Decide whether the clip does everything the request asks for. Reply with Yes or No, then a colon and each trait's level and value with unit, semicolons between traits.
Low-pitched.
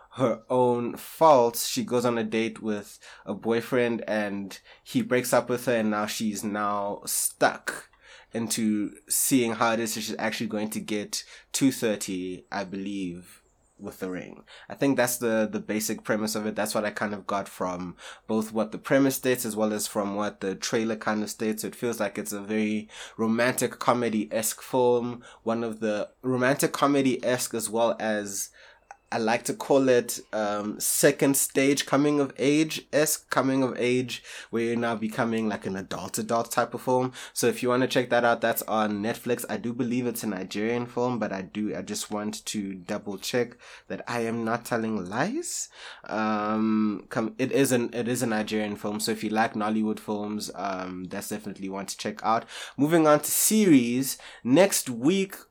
Yes: low, 115 Hz